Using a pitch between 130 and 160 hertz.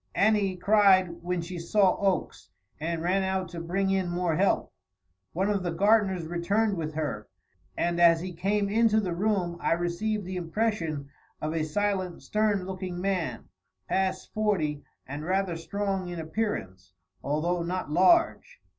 No: medium, 185 Hz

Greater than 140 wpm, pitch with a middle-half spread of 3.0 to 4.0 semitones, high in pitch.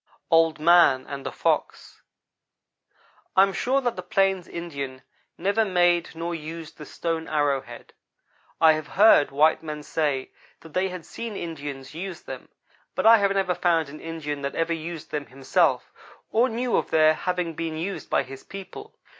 No: average, 170 wpm; average, 3.7 semitones; medium, 165 Hz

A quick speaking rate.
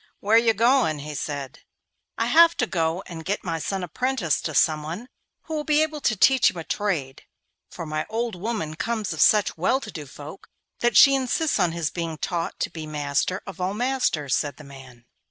Yes: fast, 210 wpm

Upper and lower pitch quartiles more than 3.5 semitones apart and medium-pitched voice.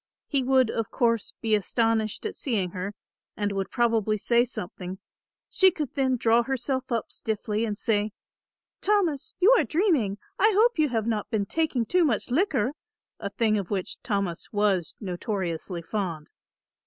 No: average, 4.6 semitones; high, 225 Hz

